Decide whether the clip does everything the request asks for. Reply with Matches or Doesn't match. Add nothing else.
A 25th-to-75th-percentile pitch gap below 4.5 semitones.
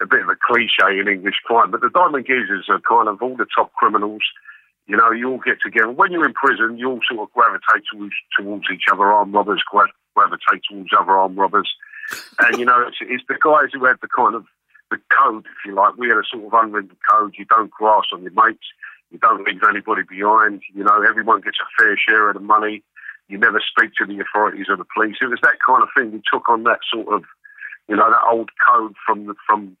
Matches